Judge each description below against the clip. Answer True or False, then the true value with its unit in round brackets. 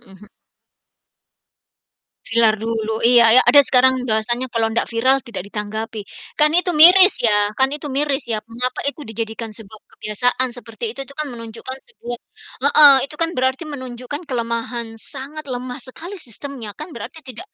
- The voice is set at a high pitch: True (245 Hz)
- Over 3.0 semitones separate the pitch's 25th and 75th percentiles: True (3.6 semitones)